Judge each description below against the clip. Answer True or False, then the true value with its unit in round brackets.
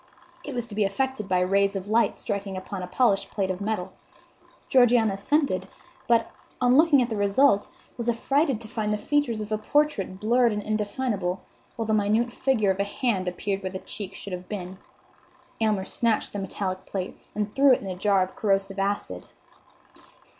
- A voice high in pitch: True (210 Hz)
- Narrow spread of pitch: False (3.4 semitones)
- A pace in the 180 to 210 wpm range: True (190 wpm)